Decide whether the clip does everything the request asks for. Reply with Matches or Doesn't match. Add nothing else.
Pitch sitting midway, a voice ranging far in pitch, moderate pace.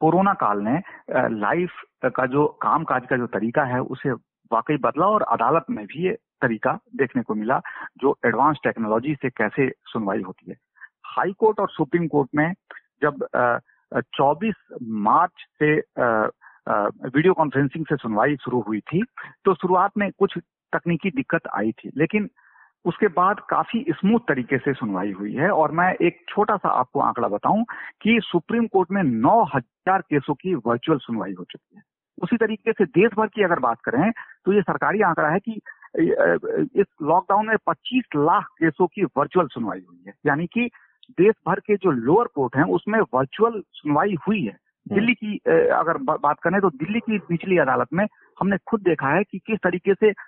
Matches